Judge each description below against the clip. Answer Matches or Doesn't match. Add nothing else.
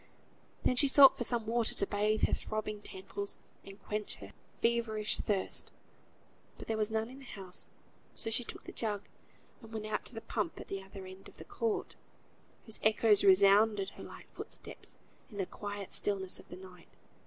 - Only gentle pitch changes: Matches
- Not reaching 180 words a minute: Doesn't match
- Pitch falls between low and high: Doesn't match